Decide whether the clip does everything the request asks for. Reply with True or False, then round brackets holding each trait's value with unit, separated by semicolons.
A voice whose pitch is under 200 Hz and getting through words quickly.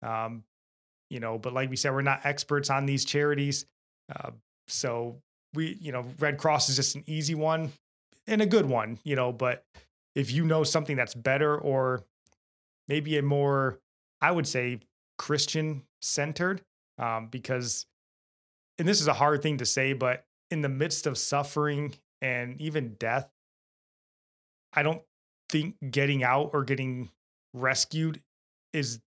False (140 Hz; 155 wpm)